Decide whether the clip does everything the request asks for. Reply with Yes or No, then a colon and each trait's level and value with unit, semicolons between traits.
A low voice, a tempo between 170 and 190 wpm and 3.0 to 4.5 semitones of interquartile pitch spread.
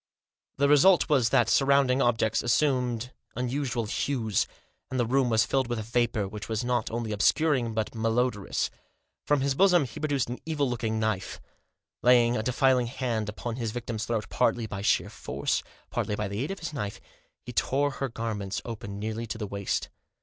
Yes: low, 120 Hz; average, 180 wpm; average, 3.3 semitones